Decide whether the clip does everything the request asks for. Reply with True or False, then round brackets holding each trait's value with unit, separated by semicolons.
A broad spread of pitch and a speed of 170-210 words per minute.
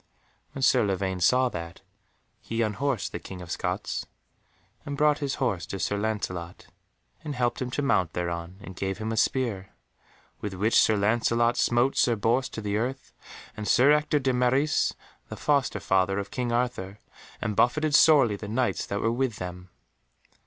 False (4.9 semitones; 175 wpm)